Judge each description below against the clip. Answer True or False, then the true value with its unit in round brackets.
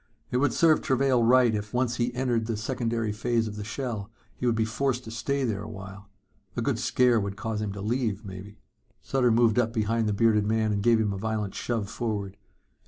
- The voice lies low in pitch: True (115 Hz)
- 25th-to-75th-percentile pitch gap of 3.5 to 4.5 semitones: False (2.6 semitones)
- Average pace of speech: False (220 wpm)